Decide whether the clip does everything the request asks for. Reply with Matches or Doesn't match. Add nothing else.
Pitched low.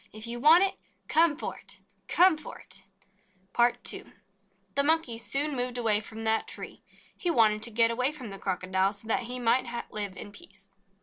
Doesn't match